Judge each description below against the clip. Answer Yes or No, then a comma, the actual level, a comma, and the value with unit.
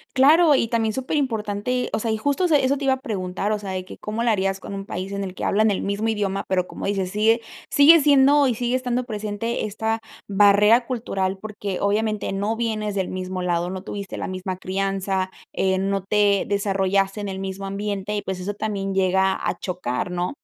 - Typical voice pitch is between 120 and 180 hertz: No, high, 205 Hz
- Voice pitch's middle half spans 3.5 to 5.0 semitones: No, average, 2.8 semitones